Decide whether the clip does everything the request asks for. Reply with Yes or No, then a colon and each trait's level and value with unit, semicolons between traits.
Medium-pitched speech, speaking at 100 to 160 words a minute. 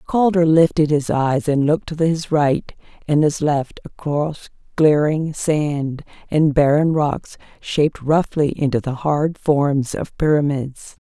Yes: medium, 150 Hz; average, 140 wpm